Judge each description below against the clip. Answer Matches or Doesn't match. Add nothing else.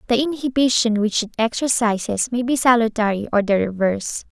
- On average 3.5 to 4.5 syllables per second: Doesn't match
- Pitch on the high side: Matches